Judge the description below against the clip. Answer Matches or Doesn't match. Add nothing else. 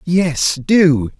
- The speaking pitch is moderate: Matches